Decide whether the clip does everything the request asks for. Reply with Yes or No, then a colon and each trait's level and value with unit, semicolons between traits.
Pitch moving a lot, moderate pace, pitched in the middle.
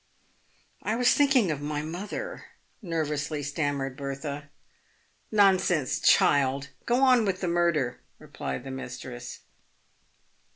No: wide, 5.8 semitones; slow, 125 wpm; medium, 150 Hz